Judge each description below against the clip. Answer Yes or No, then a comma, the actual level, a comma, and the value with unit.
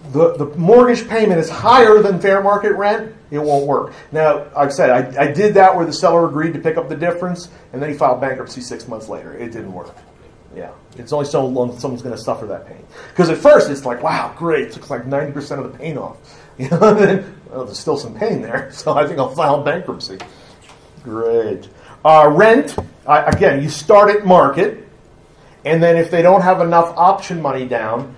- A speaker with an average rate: No, fast, 215 wpm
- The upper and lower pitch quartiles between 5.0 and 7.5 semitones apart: Yes, wide, 5.4 semitones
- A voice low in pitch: No, medium, 160 Hz